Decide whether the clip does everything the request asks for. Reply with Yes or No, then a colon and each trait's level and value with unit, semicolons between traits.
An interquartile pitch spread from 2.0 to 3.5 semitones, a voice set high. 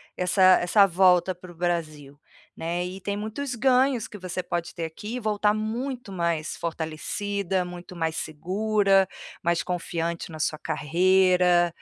No: average, 3.2 semitones; medium, 180 Hz